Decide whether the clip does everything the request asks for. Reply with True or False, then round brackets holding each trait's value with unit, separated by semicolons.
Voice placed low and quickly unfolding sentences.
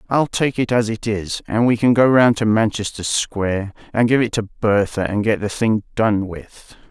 True (110 Hz; 215 wpm)